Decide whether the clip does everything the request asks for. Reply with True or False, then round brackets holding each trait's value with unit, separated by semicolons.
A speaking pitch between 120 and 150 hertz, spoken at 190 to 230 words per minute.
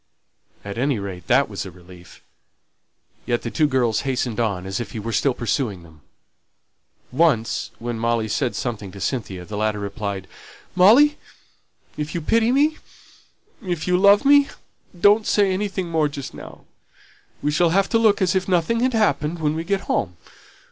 False (140 Hz; 170 wpm)